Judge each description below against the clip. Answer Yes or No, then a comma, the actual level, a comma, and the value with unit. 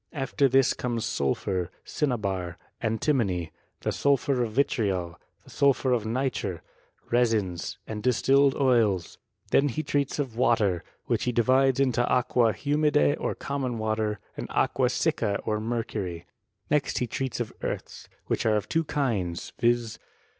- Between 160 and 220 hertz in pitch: No, low, 120 Hz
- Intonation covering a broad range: No, average, 4.2 semitones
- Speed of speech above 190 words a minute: No, average, 145 wpm